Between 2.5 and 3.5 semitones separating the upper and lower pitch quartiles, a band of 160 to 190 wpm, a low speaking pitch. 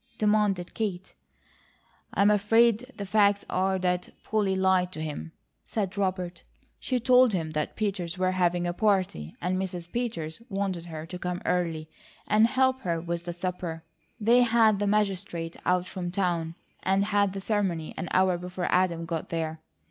No: average, 3.0 semitones; average, 165 wpm; medium, 185 Hz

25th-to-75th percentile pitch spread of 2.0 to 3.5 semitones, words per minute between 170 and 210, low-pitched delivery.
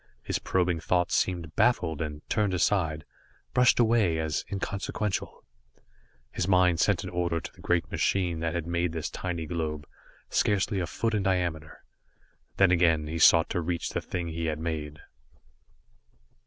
No: narrow, 2.5 semitones; average, 155 wpm; very low, 85 Hz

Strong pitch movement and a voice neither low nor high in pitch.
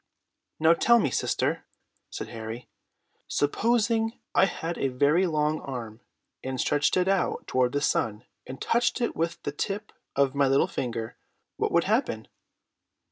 Yes: wide, 6.8 semitones; medium, 145 Hz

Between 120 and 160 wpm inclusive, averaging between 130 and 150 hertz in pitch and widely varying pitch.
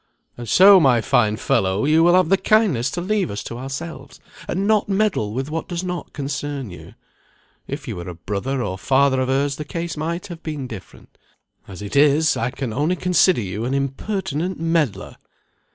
No: average, 190 wpm; medium, 140 Hz; wide, 6.1 semitones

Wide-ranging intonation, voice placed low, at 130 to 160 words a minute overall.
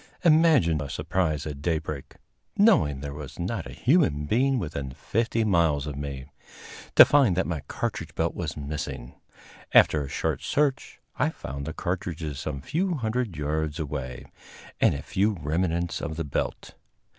Yes: wide, 7.0 semitones; very low, 80 Hz; average, 155 wpm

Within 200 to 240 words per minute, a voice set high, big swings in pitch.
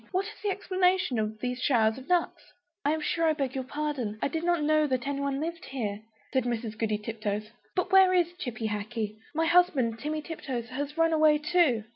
Yes: fast, 205 wpm; very high, 280 Hz; wide, 6.2 semitones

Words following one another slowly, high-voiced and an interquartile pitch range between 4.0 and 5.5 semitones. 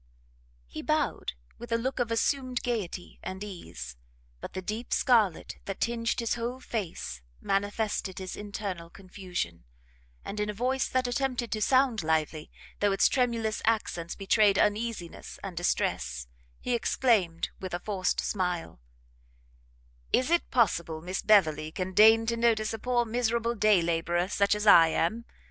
No: average, 150 wpm; high, 210 Hz; average, 4.6 semitones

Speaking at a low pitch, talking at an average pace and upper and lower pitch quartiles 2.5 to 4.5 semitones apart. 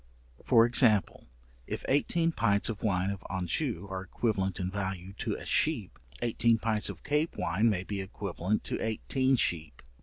Yes: low, 105 Hz; average, 160 wpm; average, 3.8 semitones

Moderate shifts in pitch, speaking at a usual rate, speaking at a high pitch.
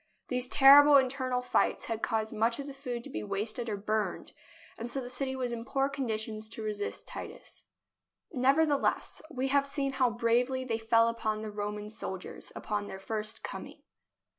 Yes: average, 3.6 semitones; average, 175 wpm; high, 235 Hz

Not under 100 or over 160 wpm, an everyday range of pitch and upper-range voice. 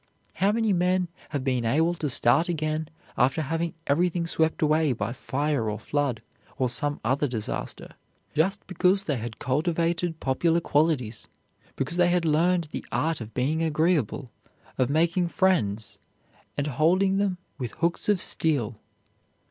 No: average, 150 wpm; average, 4.9 semitones; medium, 155 Hz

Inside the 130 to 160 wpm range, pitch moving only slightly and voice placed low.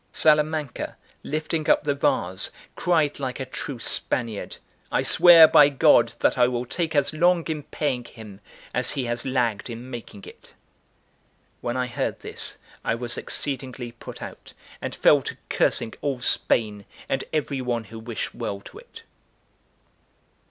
No: average, 155 wpm; average, 4.2 semitones; low, 130 Hz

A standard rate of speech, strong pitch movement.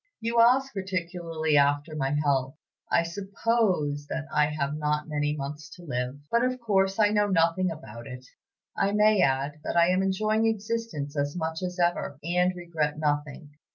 No: average, 170 wpm; average, 4.8 semitones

